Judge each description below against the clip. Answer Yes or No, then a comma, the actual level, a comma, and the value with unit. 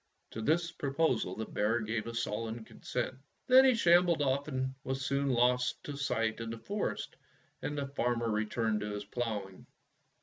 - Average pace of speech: Yes, average, 175 wpm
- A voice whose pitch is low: Yes, low, 125 Hz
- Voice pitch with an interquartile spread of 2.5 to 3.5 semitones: No, average, 4.1 semitones